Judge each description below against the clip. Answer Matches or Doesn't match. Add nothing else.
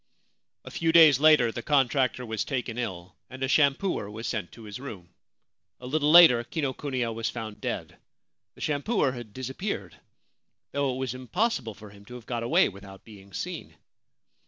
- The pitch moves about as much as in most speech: Matches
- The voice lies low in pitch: Matches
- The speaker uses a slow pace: Doesn't match